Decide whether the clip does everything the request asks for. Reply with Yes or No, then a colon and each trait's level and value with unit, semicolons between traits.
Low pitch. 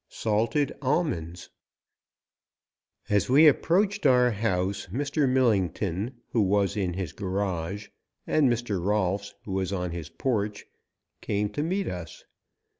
Yes: low, 105 Hz